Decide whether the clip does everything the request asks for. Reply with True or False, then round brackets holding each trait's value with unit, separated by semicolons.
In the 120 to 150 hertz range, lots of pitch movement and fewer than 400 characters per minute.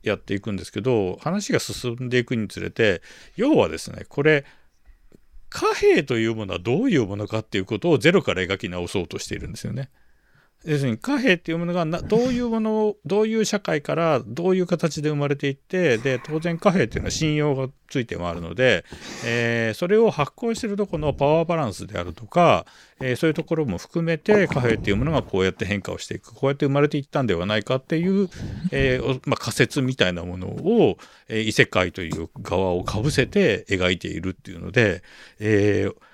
False (135 Hz; 7.7 semitones; 420 characters per minute)